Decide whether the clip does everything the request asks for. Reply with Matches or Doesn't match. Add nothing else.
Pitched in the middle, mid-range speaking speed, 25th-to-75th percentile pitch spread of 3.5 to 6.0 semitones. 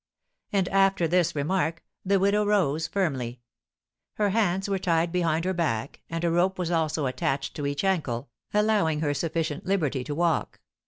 Matches